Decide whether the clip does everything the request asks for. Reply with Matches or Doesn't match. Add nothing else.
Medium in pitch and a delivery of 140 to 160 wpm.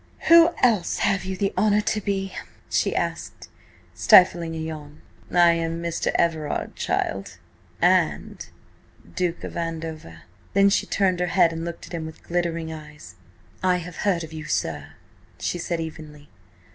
Matches